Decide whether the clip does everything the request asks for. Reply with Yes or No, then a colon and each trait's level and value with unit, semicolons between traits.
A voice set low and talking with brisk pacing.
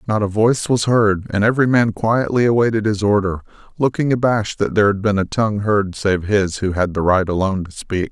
Yes: low, 105 Hz; fast, 220 wpm